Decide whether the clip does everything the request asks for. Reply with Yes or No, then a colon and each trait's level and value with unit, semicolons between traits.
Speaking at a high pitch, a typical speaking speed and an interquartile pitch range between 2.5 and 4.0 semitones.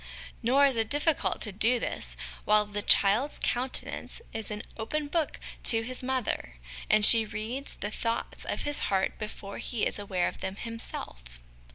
Yes: high, 225 Hz; average, 175 wpm; average, 3.7 semitones